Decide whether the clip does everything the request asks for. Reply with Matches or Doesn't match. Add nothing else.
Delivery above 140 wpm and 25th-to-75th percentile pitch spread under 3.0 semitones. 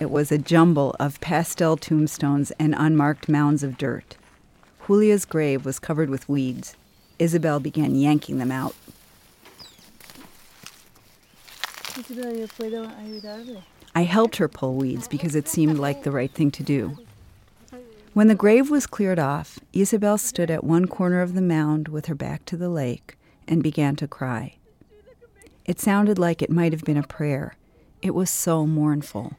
Doesn't match